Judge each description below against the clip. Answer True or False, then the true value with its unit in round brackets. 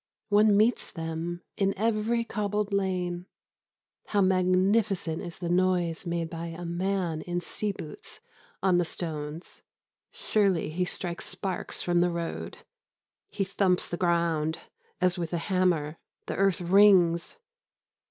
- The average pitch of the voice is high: False (180 Hz)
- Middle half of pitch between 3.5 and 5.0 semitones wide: False (2.5 semitones)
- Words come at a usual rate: False (130 wpm)